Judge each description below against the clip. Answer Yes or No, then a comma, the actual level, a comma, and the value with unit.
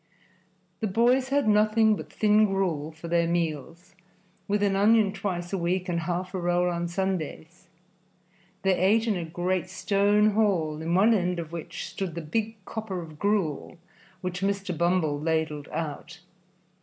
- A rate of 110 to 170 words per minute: Yes, average, 160 wpm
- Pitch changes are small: No, average, 3.4 semitones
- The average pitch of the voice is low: No, medium, 185 Hz